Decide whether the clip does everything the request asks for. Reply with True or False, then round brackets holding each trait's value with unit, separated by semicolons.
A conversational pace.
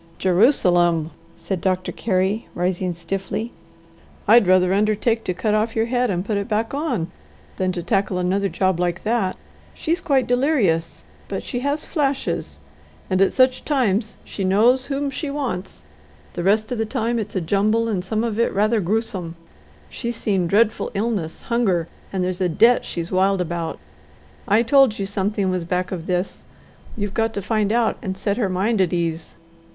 True (180 wpm)